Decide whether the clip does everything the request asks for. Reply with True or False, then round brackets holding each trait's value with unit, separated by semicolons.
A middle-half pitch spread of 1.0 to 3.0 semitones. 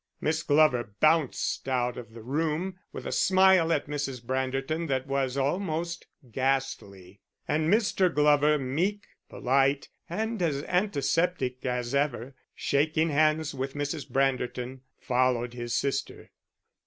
False (3.8 semitones)